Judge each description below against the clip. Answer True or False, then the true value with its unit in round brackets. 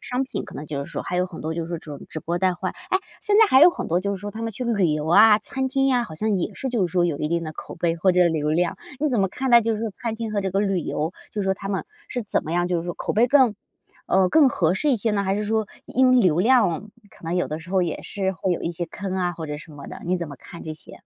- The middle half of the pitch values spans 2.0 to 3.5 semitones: False (4.9 semitones)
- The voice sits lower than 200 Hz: True (190 Hz)